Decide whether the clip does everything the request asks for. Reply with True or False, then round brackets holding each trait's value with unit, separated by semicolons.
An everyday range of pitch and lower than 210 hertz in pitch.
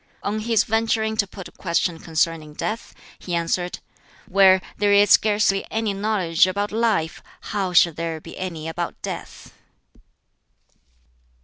True (4.1 semitones; 190 Hz)